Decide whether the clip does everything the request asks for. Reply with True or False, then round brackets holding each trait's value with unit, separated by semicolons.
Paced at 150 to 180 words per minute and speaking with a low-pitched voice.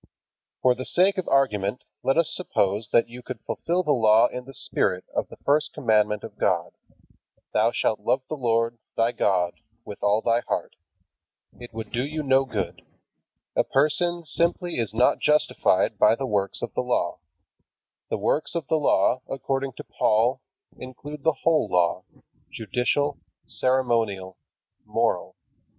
True (155 wpm; 125 Hz)